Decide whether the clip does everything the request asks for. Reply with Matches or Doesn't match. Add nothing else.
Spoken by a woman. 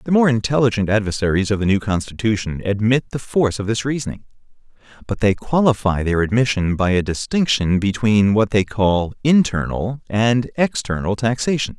Doesn't match